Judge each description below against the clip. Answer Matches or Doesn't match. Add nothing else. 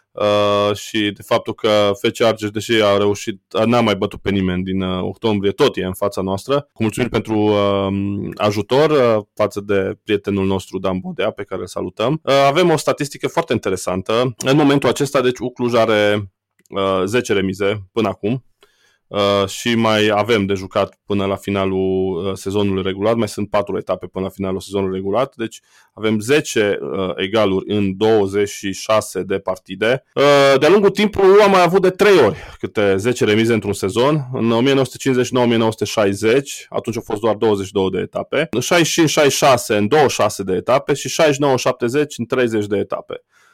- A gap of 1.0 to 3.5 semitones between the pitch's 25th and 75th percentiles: Doesn't match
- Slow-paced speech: Doesn't match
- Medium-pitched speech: Doesn't match